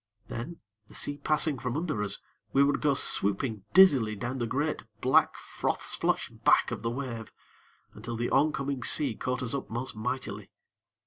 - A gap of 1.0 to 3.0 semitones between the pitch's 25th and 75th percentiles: No, average, 3.6 semitones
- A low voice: Yes, low, 125 Hz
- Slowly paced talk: No, average, 170 wpm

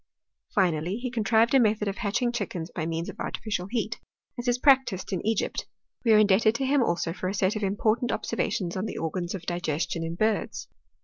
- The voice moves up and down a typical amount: Yes, average, 4.5 semitones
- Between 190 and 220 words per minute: Yes, fast, 205 wpm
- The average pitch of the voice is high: Yes, high, 205 Hz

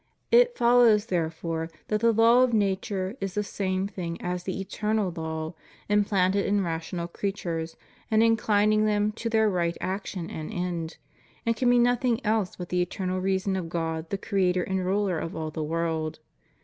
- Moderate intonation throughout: Yes, average, 3.9 semitones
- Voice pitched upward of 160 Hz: Yes, high, 190 Hz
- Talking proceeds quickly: No, average, 175 wpm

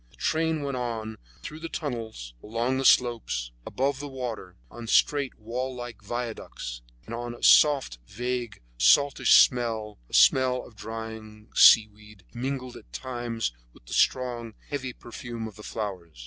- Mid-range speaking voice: No, low, 120 Hz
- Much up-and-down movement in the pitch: No, average, 3.0 semitones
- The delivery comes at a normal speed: Yes, average, 150 wpm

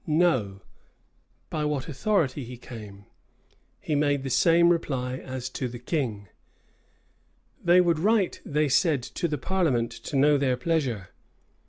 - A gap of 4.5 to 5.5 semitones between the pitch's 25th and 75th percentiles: Yes, average, 4.8 semitones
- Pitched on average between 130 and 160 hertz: Yes, medium, 140 Hz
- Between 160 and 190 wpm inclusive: No, average, 140 wpm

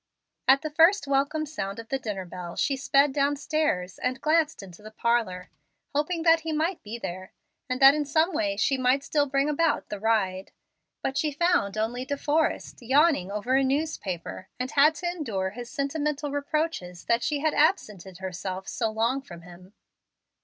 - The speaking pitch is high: Yes, very high, 270 Hz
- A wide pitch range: Yes, wide, 6.6 semitones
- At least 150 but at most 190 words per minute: Yes, average, 180 wpm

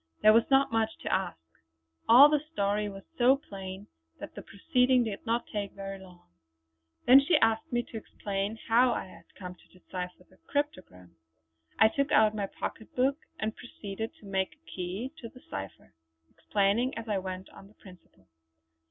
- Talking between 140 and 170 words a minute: No, average, 180 wpm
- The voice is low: No, high, 210 Hz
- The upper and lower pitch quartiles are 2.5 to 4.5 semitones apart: Yes, average, 4.2 semitones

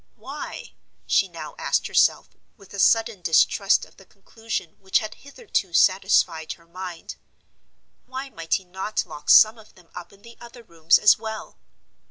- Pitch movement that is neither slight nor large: Yes, average, 4.2 semitones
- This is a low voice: No, high, 195 Hz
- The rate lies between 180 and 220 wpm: No, average, 155 wpm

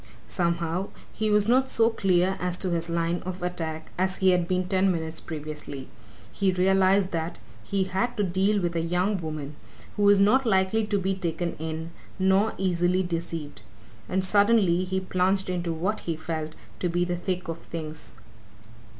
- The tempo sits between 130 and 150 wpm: No, average, 175 wpm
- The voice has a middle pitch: Yes, medium, 180 Hz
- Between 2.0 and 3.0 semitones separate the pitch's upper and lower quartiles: Yes, narrow, 2.4 semitones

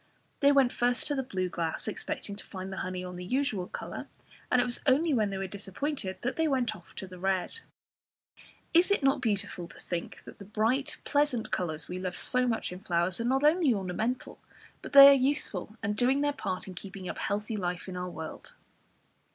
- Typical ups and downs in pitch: No, wide, 6.3 semitones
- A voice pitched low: No, high, 210 Hz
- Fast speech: Yes, fast, 215 wpm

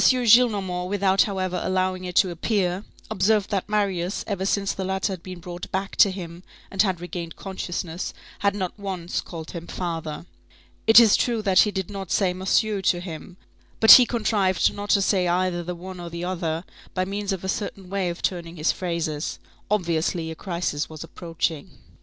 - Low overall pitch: No, medium, 185 Hz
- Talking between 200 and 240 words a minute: No, average, 185 wpm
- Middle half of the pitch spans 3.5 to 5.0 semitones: No, narrow, 2.4 semitones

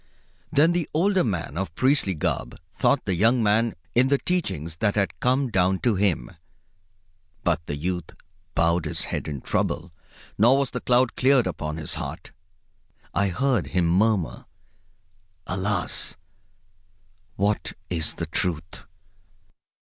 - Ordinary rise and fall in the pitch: No, wide, 7.0 semitones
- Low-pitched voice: Yes, low, 100 Hz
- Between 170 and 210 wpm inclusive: No, slow, 135 wpm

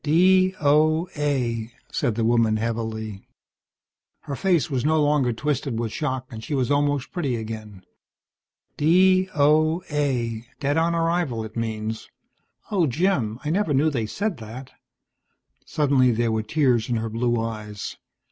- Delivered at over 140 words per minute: No, slow, 135 wpm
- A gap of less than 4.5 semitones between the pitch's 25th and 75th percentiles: No, wide, 5.6 semitones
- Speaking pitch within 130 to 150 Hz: Yes, low, 135 Hz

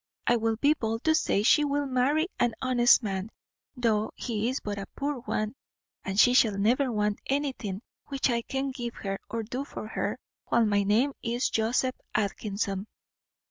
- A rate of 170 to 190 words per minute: Yes, average, 180 wpm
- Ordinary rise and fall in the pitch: Yes, average, 3.8 semitones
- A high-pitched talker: Yes, high, 235 Hz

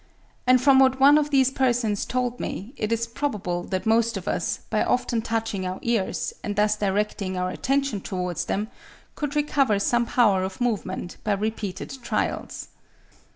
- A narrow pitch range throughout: No, average, 4.4 semitones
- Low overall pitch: No, high, 225 Hz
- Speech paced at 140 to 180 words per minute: Yes, average, 165 wpm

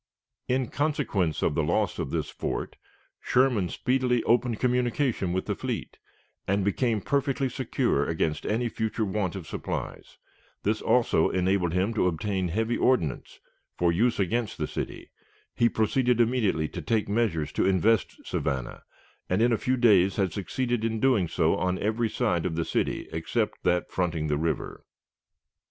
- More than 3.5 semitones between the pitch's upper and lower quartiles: Yes, average, 5.1 semitones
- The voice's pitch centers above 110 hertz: No, low, 105 Hz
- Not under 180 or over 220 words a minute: No, average, 160 wpm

